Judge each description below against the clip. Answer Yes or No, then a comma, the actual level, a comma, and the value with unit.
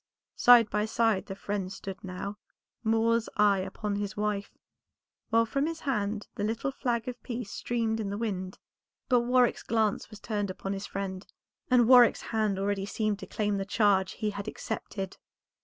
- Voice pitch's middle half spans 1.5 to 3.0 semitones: Yes, narrow, 2.6 semitones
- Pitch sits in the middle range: No, high, 210 Hz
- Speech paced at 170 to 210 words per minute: Yes, average, 175 wpm